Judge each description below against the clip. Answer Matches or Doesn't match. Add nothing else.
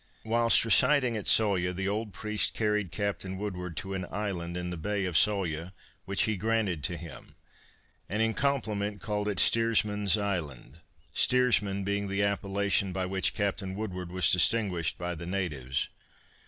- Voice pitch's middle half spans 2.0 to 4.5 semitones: Matches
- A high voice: Doesn't match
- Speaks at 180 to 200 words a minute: Doesn't match